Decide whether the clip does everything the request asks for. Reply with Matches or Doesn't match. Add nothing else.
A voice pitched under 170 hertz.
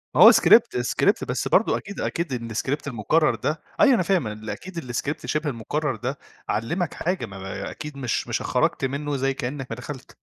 Matches